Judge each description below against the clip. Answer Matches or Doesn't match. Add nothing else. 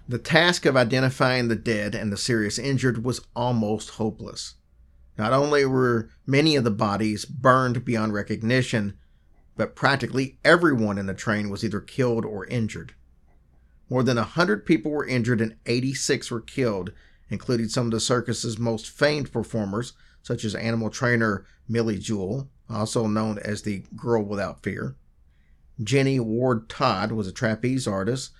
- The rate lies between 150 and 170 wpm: Matches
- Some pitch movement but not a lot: Matches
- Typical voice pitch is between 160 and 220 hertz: Doesn't match